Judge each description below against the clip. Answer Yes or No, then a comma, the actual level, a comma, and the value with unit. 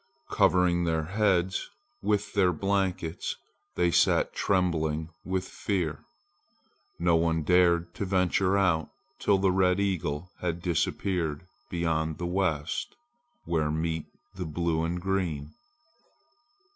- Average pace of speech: No, slow, 115 wpm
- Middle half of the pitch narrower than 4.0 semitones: Yes, narrow, 2.5 semitones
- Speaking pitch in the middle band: No, very low, 85 Hz